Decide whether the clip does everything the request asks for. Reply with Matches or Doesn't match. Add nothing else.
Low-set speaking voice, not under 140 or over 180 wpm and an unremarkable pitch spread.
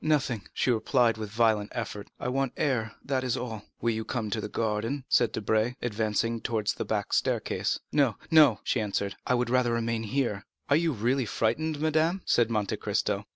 Doesn't match